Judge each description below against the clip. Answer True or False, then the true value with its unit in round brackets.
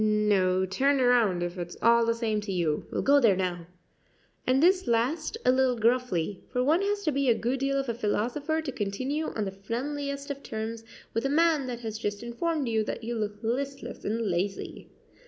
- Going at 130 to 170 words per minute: False (205 wpm)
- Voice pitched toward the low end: False (235 Hz)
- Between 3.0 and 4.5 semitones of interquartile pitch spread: False (4.9 semitones)